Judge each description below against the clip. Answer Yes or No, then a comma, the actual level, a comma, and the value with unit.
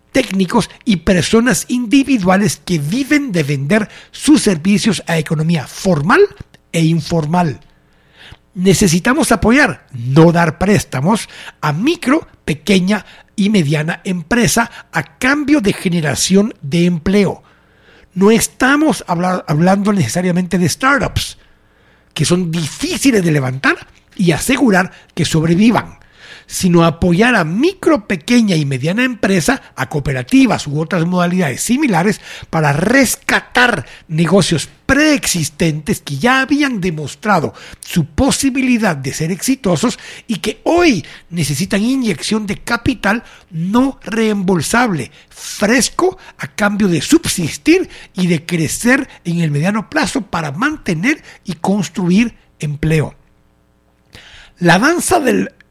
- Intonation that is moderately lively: No, wide, 6.4 semitones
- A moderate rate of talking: No, slow, 110 wpm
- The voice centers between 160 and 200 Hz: Yes, high, 190 Hz